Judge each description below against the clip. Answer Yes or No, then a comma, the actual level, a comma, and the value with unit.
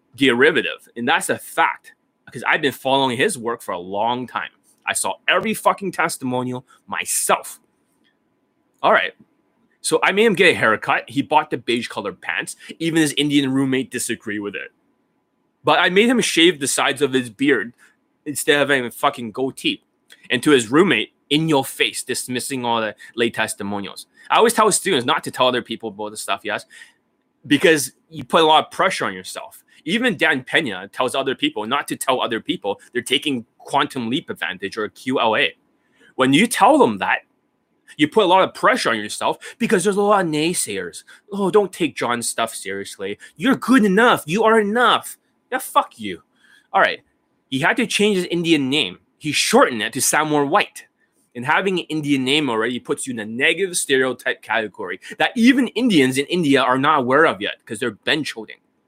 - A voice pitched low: No, medium, 150 Hz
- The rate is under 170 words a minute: No, average, 195 wpm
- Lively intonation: Yes, wide, 9.0 semitones